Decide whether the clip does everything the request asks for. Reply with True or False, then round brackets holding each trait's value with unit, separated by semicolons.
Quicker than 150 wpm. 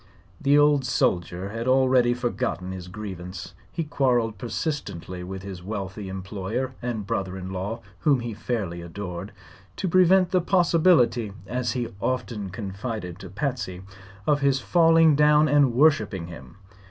False (140 wpm)